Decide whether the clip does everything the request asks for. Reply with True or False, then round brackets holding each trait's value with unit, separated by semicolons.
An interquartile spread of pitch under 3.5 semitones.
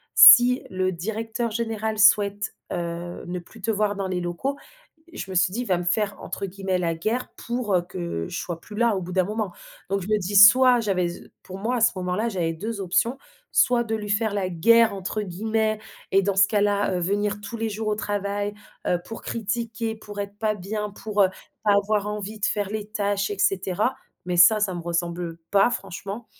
True (2.9 semitones)